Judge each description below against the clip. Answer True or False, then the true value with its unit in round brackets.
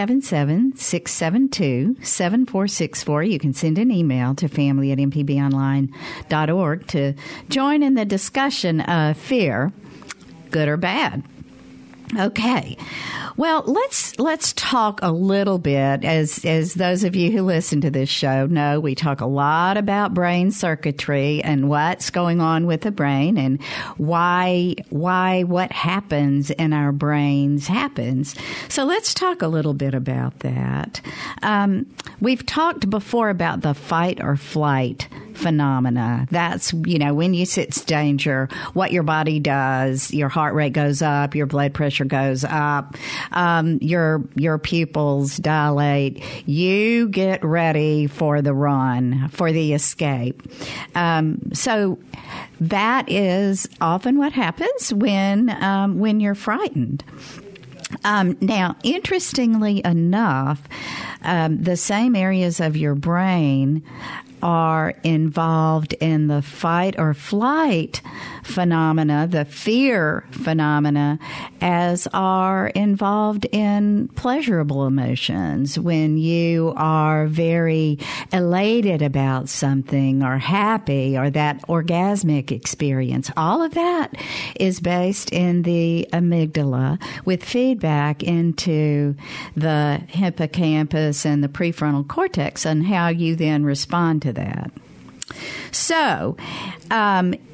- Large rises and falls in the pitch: False (4.8 semitones)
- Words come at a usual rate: False (120 wpm)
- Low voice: False (160 Hz)